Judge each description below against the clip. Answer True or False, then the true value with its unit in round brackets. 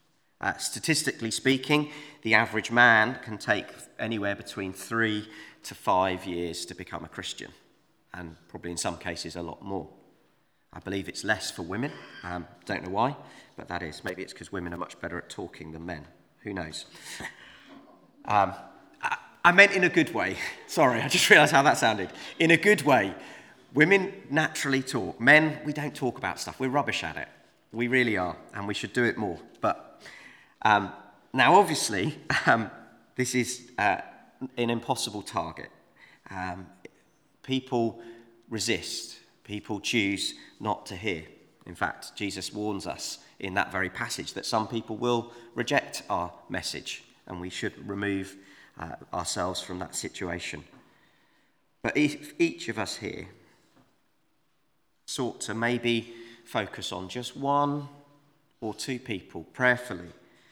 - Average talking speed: True (155 wpm)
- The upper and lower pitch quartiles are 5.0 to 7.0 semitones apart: True (5.3 semitones)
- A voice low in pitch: True (115 Hz)